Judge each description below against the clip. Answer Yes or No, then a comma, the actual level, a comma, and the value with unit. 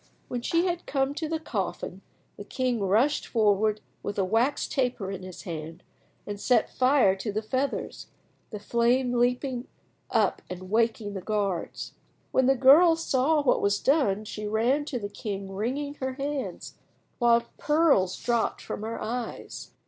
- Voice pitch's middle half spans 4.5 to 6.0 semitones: Yes, average, 4.8 semitones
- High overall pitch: Yes, high, 235 Hz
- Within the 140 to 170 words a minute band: Yes, average, 160 wpm